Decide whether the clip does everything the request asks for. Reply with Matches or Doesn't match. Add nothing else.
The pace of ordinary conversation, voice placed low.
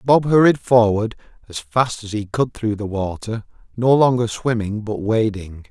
Matches